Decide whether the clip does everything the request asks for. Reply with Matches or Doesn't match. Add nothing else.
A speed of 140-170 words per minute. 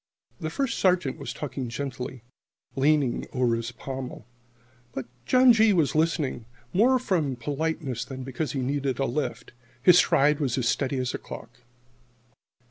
Matches